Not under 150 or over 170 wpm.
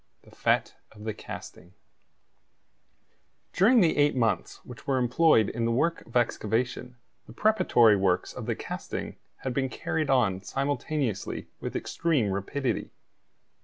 No: slow, 135 wpm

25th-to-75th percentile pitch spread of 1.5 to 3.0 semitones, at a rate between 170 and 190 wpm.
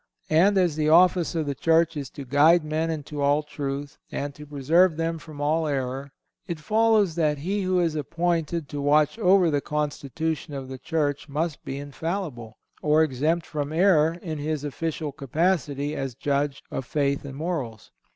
Yes: average, 2.7 semitones; average, 175 wpm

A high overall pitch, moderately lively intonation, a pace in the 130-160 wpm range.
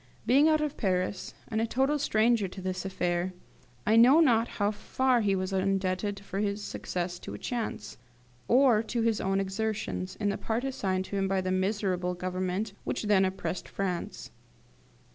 No: high, 200 Hz; average, 3.4 semitones; average, 170 wpm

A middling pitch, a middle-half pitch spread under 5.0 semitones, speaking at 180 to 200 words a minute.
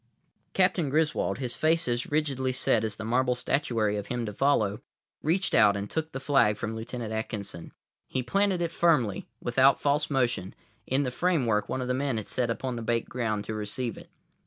No: low, 125 Hz; average, 4.4 semitones; average, 195 wpm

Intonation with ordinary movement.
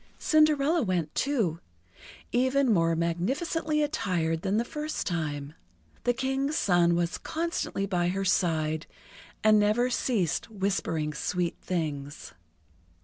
No: wide, 8.1 semitones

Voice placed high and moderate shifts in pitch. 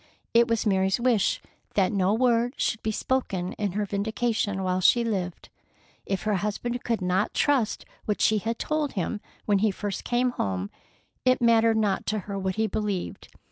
Yes: high, 210 Hz; average, 3.3 semitones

